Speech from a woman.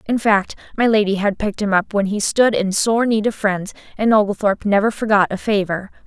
Yes: female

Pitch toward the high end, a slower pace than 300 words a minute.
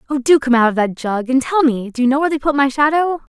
No: very high, 270 Hz; fast, 320 wpm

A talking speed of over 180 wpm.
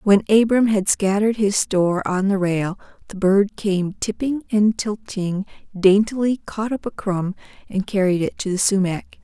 No: average, 170 wpm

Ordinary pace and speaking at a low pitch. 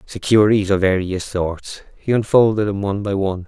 Yes: average, 175 wpm; low, 100 Hz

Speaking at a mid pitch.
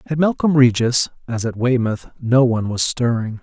No: low, 125 Hz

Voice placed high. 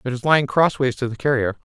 No: low, 130 Hz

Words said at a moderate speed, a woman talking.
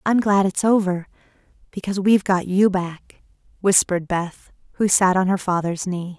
Yes: average, 165 wpm; female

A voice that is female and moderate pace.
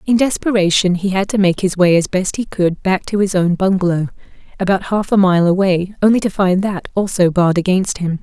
No: female; fast, 220 wpm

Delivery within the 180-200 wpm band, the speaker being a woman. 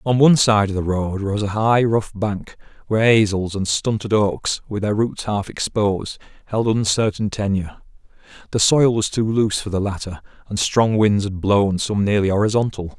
No: average, 185 wpm; male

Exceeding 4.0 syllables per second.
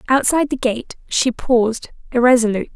Yes: 5.8 syllables/s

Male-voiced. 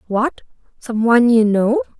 No: female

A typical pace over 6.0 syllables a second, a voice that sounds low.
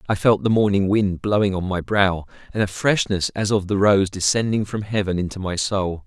No: 5.2 syllables/s; low, 100 Hz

